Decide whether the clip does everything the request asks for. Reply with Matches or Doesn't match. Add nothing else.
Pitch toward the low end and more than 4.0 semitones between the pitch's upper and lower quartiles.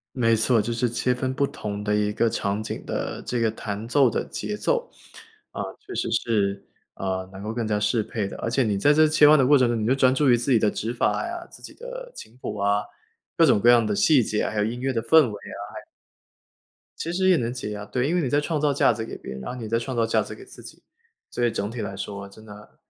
Matches